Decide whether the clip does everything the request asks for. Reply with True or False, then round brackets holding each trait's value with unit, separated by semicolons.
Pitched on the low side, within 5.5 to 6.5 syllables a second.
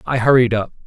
True (120 Hz; 6.3 syllables/s)